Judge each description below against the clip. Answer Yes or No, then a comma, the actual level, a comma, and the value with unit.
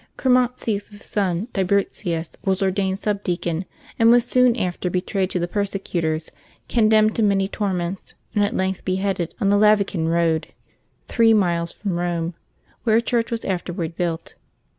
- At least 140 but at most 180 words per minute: Yes, average, 145 wpm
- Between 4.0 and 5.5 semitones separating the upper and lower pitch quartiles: No, average, 3.4 semitones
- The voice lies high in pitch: Yes, high, 195 Hz